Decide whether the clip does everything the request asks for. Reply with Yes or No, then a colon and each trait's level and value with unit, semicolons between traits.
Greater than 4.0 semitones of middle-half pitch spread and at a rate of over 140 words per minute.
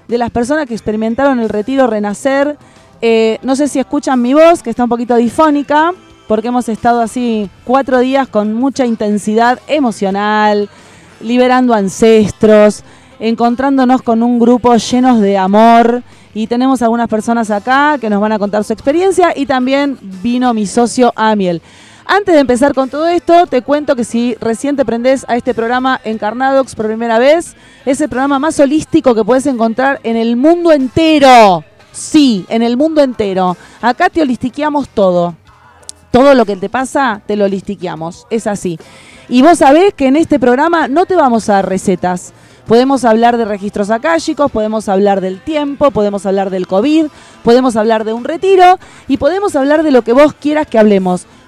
Yes: average, 4.4 semitones; average, 175 wpm